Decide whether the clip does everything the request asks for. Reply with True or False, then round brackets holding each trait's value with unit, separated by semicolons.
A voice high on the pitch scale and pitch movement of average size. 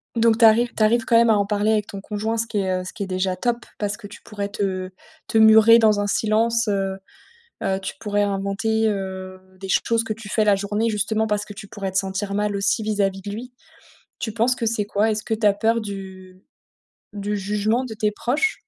False (210 Hz; 2.0 semitones)